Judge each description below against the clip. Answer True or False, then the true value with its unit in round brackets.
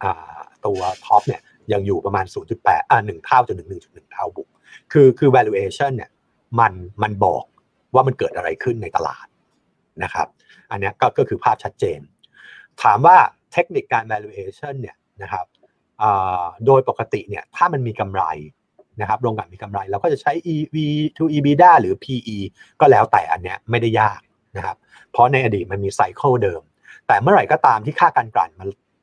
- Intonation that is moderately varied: False (8.9 semitones)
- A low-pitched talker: True (130 Hz)